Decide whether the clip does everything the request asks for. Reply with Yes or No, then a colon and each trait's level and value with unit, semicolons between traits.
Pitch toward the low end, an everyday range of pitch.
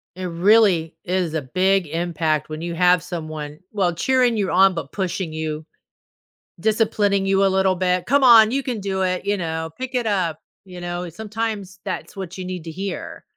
No: medium, 185 Hz; average, 3.2 semitones